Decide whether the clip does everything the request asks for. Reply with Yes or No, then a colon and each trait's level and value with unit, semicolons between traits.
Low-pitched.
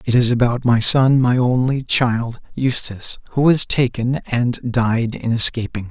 Yes: low, 120 Hz